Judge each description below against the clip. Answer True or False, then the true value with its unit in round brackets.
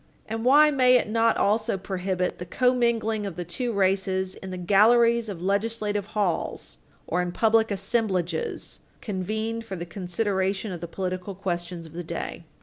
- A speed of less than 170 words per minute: True (160 wpm)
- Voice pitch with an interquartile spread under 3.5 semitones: False (3.8 semitones)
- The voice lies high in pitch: True (195 Hz)